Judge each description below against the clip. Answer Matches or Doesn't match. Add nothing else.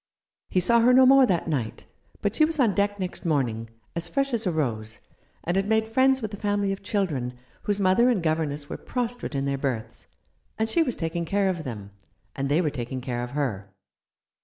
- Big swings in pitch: Matches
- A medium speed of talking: Doesn't match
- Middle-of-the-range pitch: Matches